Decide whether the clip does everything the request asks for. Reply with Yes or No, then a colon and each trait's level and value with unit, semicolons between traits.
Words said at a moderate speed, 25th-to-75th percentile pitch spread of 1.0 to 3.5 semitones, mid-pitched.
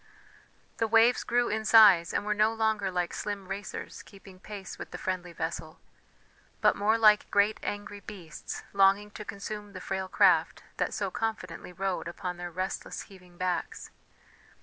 No: average, 160 wpm; narrow, 2.5 semitones; high, 200 Hz